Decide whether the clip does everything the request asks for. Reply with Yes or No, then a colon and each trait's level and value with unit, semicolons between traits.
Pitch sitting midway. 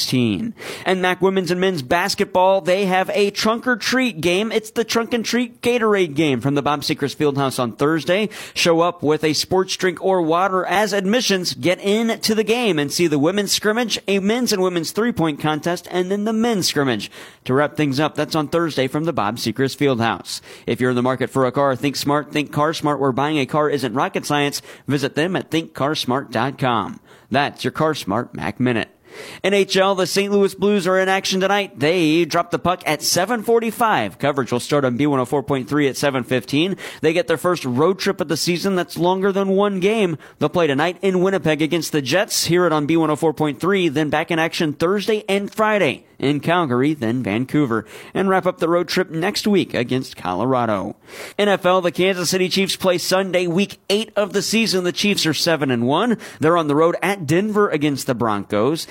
Yes: medium, 170 Hz